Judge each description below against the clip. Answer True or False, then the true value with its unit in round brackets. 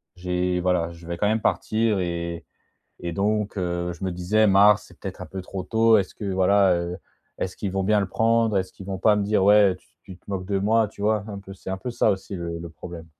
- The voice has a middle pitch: False (95 Hz)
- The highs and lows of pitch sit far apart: False (2.7 semitones)